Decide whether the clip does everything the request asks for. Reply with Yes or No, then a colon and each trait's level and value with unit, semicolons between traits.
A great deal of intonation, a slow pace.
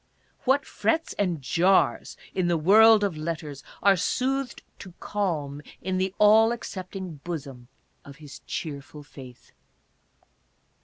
Yes: wide, 5.7 semitones; slow, 120 wpm